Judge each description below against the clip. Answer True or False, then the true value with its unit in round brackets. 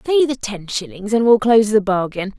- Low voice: False (215 Hz)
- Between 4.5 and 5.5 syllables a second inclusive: True (5.4 syllables/s)